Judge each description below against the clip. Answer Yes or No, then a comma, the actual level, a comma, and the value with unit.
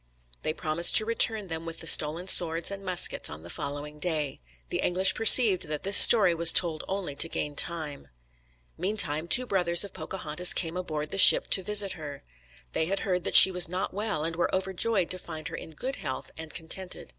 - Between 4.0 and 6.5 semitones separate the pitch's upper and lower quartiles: No, average, 3.5 semitones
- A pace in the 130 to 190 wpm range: No, fast, 205 wpm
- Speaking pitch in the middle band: Yes, medium, 170 Hz